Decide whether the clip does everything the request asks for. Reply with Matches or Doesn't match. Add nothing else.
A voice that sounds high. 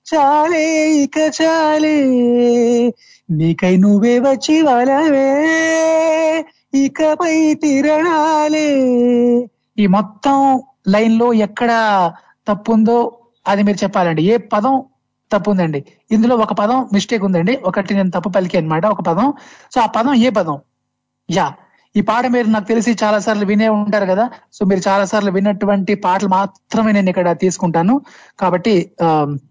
Matches